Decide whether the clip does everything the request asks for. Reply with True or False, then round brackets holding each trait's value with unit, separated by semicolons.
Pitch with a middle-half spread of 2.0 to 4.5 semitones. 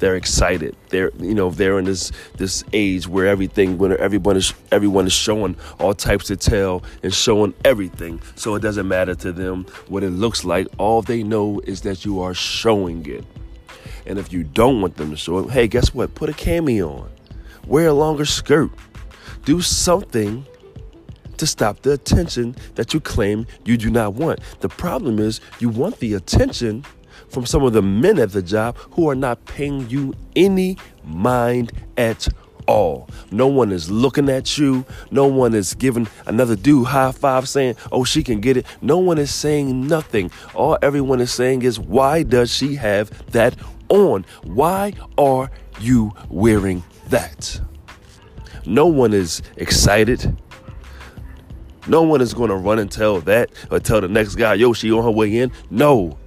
False (5.1 semitones)